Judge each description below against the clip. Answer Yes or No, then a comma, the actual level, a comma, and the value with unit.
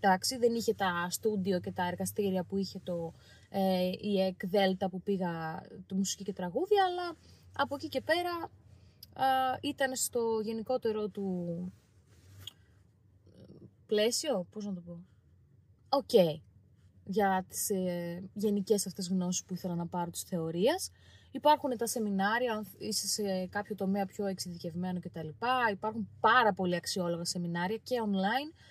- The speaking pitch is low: No, high, 195 Hz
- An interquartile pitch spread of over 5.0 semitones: No, average, 4.0 semitones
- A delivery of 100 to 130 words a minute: No, average, 140 wpm